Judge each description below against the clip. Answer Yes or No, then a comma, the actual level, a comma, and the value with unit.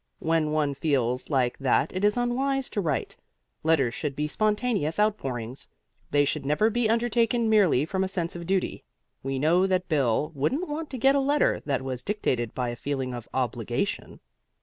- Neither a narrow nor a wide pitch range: No, wide, 8.1 semitones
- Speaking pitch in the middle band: Yes, medium, 160 Hz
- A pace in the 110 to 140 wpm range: No, average, 180 wpm